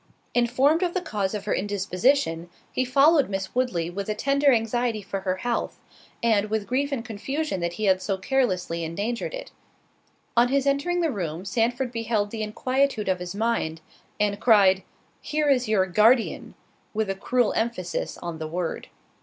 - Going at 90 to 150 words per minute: No, average, 170 wpm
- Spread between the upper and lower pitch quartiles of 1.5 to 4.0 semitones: No, average, 5.1 semitones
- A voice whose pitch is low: No, high, 220 Hz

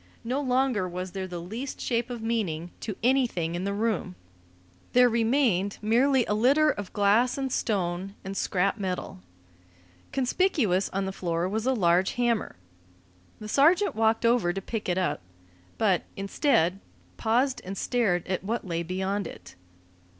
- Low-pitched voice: No, high, 210 Hz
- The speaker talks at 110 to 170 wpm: Yes, average, 155 wpm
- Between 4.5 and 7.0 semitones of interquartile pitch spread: Yes, average, 4.9 semitones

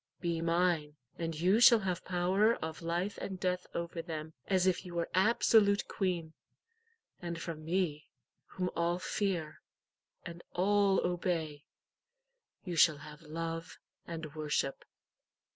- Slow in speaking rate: Yes, slow, 130 wpm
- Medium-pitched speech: Yes, medium, 170 Hz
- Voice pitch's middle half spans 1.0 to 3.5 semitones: Yes, narrow, 2.4 semitones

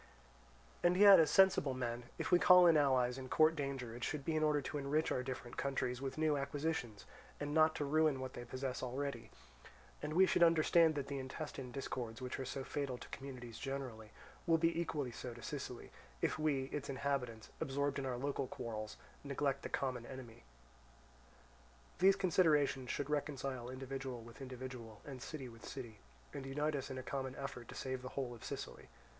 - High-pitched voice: No, low, 135 Hz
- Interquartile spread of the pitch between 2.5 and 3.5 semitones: Yes, average, 2.8 semitones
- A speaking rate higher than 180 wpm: Yes, average, 190 wpm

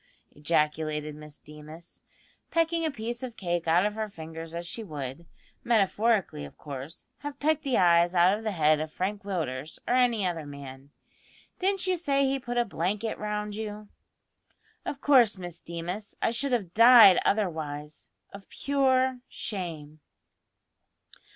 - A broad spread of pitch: Yes, wide, 7.0 semitones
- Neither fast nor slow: Yes, average, 150 wpm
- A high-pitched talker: Yes, high, 195 Hz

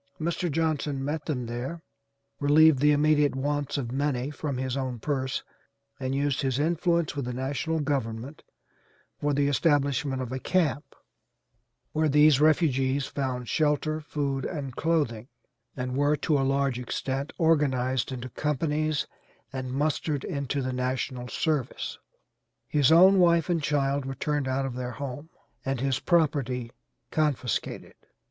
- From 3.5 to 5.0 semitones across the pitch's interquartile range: No, narrow, 2.6 semitones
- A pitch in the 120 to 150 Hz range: Yes, medium, 140 Hz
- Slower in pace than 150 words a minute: Yes, average, 140 wpm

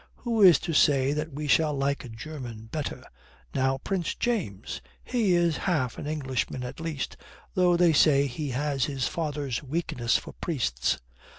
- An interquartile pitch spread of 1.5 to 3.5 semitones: No, average, 4.0 semitones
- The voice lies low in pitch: No, medium, 145 Hz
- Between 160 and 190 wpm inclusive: Yes, average, 165 wpm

